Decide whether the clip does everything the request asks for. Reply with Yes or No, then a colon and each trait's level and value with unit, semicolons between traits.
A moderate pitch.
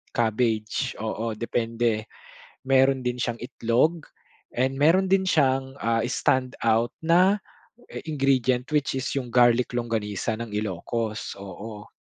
No: low, 120 Hz